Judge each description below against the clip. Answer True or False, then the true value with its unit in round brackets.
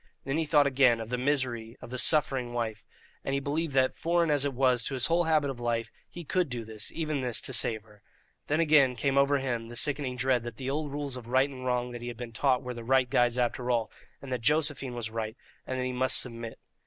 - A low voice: True (130 Hz)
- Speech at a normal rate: False (255 wpm)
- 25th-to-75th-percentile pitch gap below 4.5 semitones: True (3.0 semitones)